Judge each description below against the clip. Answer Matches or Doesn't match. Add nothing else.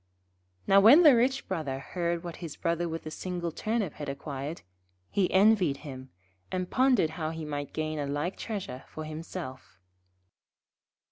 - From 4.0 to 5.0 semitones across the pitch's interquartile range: Matches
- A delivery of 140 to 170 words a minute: Matches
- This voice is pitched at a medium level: Matches